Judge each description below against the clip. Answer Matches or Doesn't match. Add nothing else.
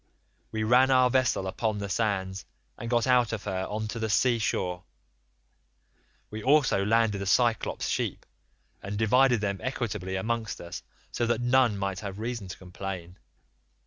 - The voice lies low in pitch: Matches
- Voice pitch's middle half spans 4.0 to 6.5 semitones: Doesn't match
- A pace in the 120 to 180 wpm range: Matches